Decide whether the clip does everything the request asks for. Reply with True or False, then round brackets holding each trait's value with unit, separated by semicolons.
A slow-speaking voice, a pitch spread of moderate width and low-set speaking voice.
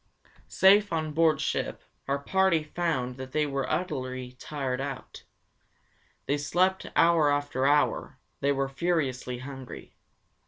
False (130 wpm; 3.9 semitones; 145 Hz)